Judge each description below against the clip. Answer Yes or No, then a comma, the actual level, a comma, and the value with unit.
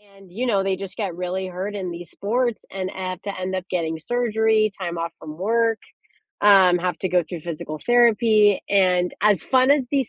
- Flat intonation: No, average, 3.5 semitones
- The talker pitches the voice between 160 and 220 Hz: Yes, high, 190 Hz